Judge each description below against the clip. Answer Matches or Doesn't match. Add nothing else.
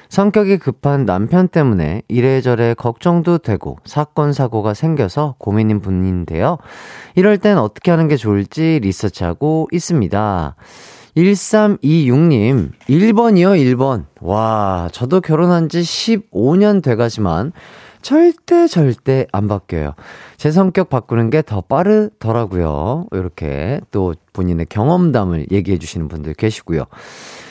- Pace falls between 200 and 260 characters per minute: Matches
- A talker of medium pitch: Doesn't match